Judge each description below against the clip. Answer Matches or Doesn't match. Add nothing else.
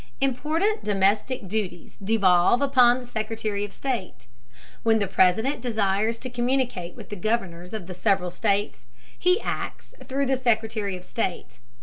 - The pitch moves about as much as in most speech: Matches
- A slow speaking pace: Doesn't match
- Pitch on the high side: Matches